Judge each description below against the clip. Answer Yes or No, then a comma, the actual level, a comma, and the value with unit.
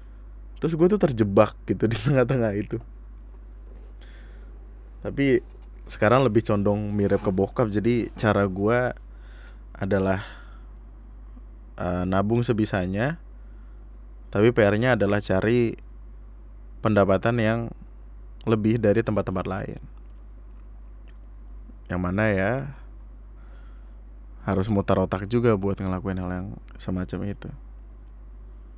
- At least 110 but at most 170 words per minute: No, average, 95 wpm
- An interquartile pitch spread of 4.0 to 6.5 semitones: No, average, 3.3 semitones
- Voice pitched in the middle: No, low, 105 Hz